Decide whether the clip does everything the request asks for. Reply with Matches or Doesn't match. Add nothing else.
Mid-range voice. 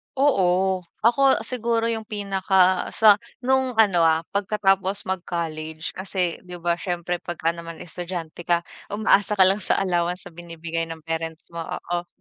Matches